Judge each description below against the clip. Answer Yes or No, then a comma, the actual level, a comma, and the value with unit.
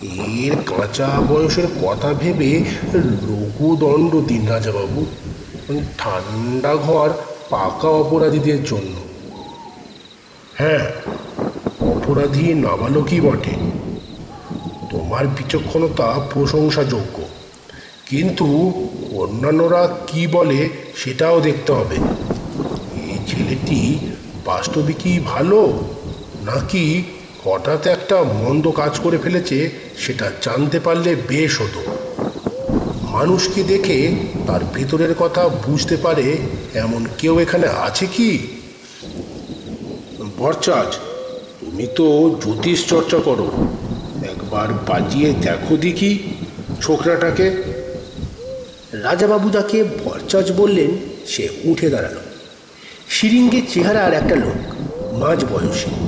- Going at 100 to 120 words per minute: No, average, 85 wpm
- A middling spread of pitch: Yes, average, 4.3 semitones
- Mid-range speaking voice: Yes, medium, 155 Hz